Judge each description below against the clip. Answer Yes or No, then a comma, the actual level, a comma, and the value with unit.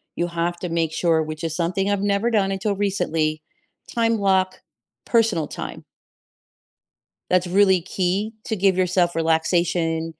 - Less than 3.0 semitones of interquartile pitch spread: No, average, 3.3 semitones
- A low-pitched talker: No, medium, 180 Hz